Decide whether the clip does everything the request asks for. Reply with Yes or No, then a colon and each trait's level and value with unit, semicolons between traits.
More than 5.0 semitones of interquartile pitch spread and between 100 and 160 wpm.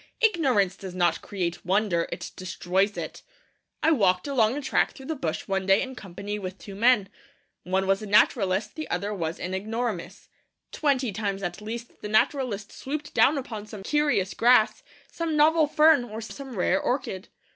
No: wide, 5.6 semitones; average, 175 wpm